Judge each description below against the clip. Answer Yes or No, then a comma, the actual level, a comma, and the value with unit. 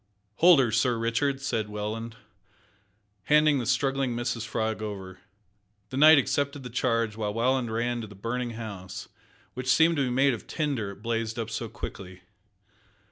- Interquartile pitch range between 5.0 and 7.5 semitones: No, average, 3.3 semitones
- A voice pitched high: No, low, 115 Hz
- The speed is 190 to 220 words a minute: No, average, 165 wpm